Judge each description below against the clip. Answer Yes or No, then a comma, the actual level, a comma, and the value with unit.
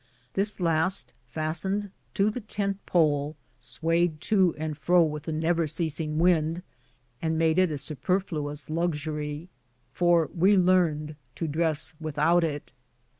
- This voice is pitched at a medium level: Yes, medium, 165 Hz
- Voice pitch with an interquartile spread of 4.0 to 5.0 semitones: No, average, 2.7 semitones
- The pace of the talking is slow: Yes, slow, 130 wpm